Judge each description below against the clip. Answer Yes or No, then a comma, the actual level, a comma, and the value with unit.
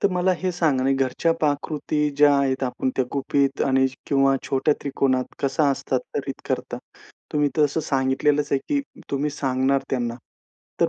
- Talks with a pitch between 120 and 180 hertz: Yes, medium, 140 Hz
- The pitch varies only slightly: Yes, narrow, 1.9 semitones